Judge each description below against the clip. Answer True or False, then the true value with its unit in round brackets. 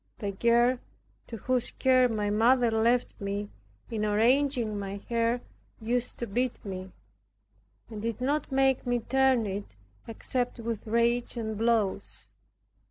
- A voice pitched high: True (235 Hz)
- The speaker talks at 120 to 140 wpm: True (135 wpm)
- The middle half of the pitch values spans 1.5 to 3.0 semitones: True (2.7 semitones)